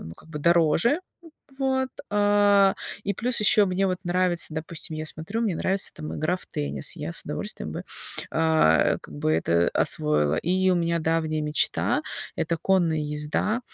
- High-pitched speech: No, medium, 170 Hz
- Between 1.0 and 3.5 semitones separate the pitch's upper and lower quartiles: No, average, 4.2 semitones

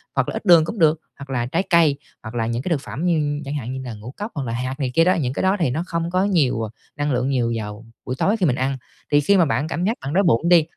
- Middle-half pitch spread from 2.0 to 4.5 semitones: No, average, 5.1 semitones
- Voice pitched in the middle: Yes, medium, 145 Hz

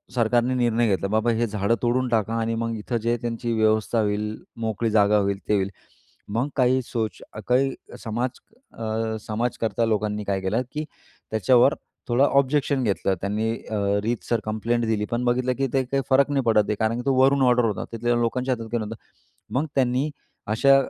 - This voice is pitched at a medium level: No, low, 115 Hz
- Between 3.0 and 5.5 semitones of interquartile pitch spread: No, narrow, 2.5 semitones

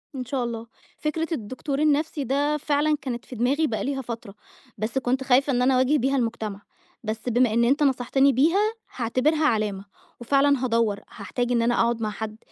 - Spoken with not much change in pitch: No, average, 3.6 semitones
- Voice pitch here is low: No, very high, 255 Hz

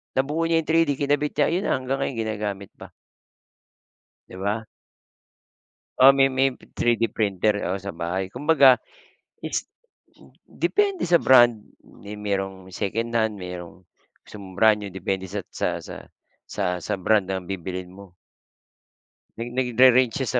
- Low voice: Yes, low, 110 Hz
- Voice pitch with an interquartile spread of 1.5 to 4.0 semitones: No, wide, 5.4 semitones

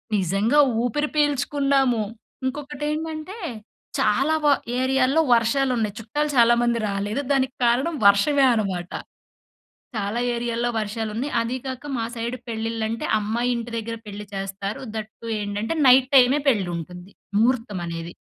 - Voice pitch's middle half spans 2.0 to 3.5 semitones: No, average, 4.2 semitones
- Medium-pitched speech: No, high, 235 Hz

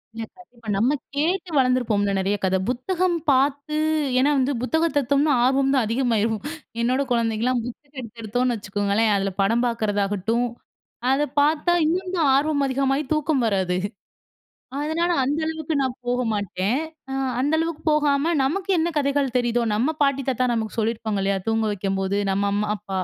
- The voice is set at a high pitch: Yes, very high, 250 Hz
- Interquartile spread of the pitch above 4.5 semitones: Yes, average, 5.0 semitones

